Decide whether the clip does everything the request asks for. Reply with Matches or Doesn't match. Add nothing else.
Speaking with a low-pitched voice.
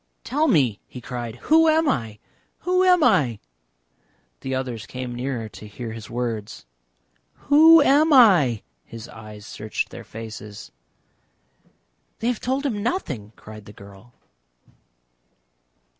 Matches